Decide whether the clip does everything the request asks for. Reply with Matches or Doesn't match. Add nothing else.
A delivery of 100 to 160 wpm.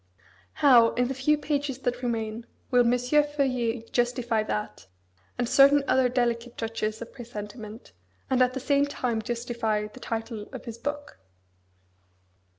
Matches